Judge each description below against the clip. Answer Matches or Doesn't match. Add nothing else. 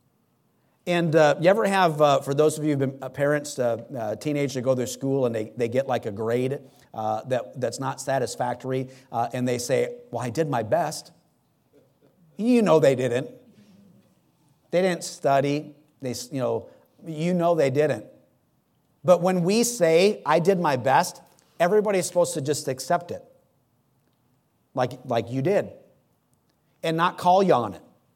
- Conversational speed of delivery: Matches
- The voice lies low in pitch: Doesn't match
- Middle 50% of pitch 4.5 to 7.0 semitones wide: Matches